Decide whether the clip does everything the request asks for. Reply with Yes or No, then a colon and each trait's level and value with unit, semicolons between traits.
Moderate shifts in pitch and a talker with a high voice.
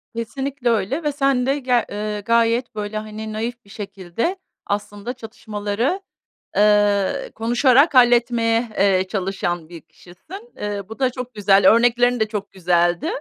Yes: average, 3.4 semitones; high, 220 Hz